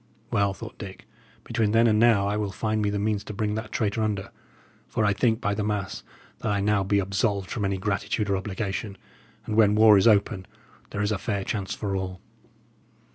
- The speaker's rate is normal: No, fast, 210 wpm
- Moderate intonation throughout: No, narrow, 1.6 semitones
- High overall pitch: No, low, 105 Hz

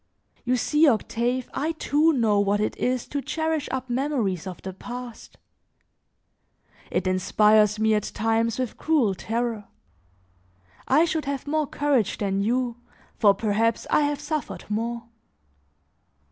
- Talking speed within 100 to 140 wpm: Yes, slow, 135 wpm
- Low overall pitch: No, high, 235 Hz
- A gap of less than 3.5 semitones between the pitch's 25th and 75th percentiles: No, average, 5.2 semitones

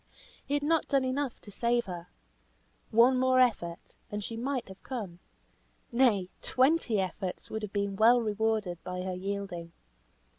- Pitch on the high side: Yes, high, 220 Hz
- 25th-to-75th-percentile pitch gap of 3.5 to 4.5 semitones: No, average, 5.0 semitones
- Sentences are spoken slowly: No, average, 155 wpm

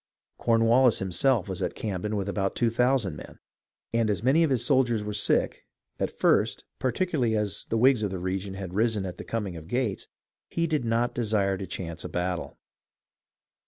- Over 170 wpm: Yes, average, 185 wpm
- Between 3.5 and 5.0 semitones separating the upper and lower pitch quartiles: Yes, average, 4.0 semitones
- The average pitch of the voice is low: Yes, low, 110 Hz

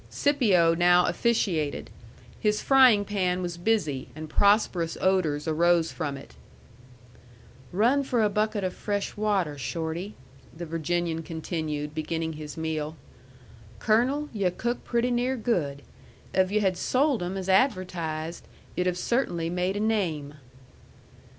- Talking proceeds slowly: Yes, slow, 130 wpm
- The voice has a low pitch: No, medium, 180 Hz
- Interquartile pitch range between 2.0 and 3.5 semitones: No, average, 4.8 semitones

